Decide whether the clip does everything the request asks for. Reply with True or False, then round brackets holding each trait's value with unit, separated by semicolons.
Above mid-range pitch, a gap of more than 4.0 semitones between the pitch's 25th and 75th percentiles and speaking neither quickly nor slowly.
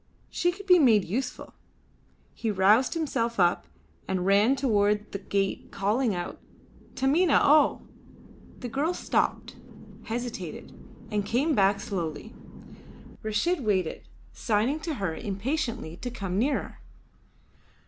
False (225 Hz; 5.5 semitones; 115 wpm)